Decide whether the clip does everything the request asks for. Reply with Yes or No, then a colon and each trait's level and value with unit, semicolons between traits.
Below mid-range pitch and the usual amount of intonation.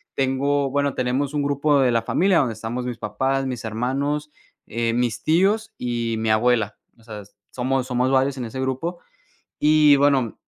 Yes: low, 130 Hz; average, 3.3 semitones